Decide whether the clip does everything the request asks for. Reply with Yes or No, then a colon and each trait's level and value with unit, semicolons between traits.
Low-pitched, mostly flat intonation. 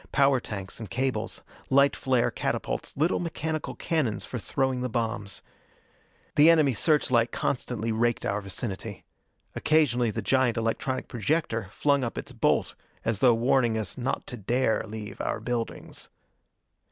No: low, 120 Hz; average, 3.3 semitones